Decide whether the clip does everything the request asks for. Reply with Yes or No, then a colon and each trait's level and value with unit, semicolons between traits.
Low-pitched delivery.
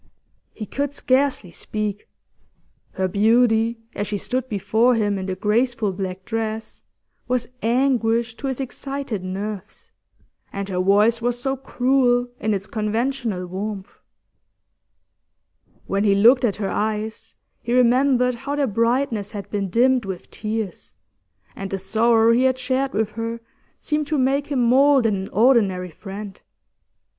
No: high, 225 Hz